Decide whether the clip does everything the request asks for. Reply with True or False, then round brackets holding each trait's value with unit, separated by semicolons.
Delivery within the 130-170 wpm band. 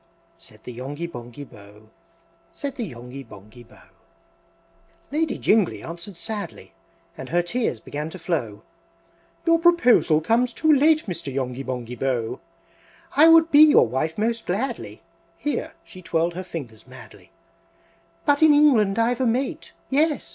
True (145 wpm)